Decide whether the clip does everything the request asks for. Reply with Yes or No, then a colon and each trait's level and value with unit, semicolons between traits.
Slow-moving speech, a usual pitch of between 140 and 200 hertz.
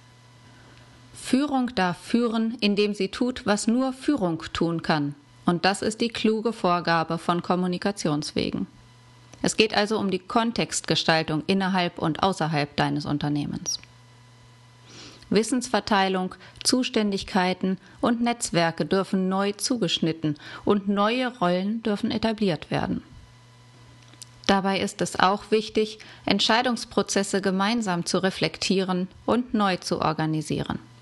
Yes: slow, 110 wpm; medium, 185 Hz